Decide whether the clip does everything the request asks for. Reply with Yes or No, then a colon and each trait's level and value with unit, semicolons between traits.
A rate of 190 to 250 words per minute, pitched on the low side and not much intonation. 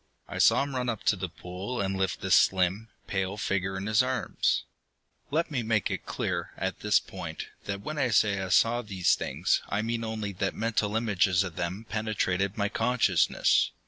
No: average, 195 wpm; low, 105 Hz; average, 3.1 semitones